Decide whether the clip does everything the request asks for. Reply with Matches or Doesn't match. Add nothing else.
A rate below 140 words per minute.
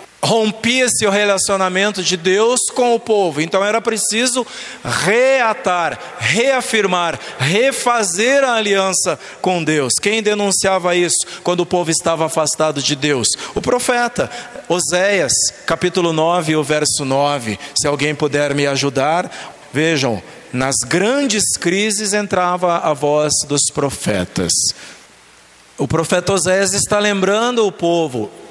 Matches